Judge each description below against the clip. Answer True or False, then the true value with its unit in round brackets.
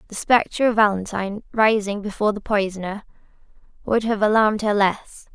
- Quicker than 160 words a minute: False (145 wpm)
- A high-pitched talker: True (210 Hz)